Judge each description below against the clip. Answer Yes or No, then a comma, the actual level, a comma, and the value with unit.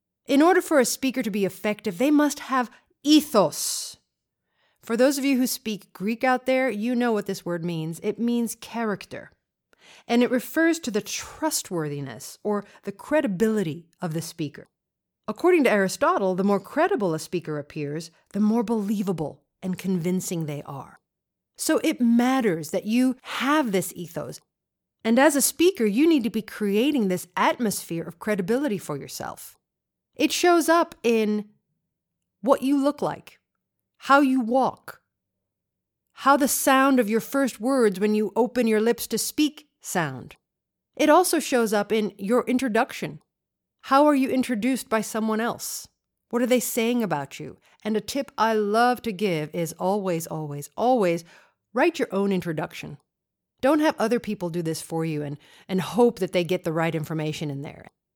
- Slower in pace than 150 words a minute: No, average, 165 wpm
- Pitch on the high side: Yes, high, 220 Hz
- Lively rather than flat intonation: Yes, wide, 6.0 semitones